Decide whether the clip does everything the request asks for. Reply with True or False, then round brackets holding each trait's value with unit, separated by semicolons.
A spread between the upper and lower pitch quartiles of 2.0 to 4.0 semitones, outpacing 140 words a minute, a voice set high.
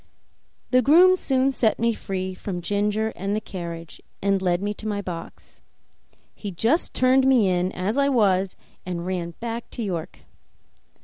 False (4.4 semitones; 165 wpm; 205 Hz)